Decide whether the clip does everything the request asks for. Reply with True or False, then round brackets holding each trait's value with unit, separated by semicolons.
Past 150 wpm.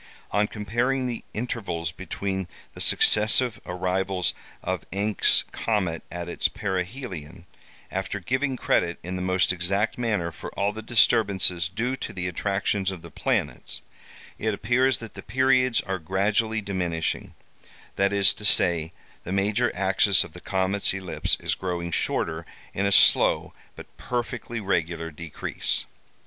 False (140 wpm)